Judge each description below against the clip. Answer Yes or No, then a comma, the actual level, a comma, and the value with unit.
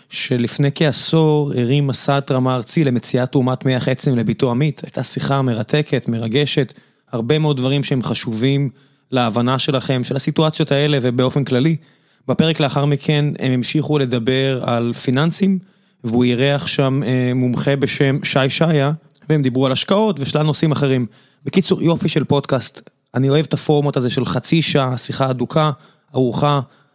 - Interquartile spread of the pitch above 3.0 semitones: No, average, 2.7 semitones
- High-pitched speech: No, medium, 140 Hz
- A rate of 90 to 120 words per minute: No, average, 145 wpm